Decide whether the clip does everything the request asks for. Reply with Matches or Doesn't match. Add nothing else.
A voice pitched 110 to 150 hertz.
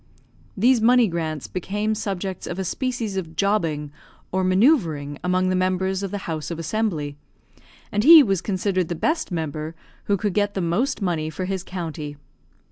Doesn't match